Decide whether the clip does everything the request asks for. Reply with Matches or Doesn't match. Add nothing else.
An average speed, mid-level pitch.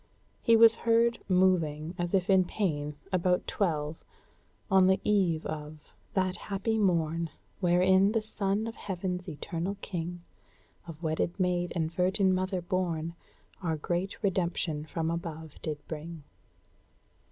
Doesn't match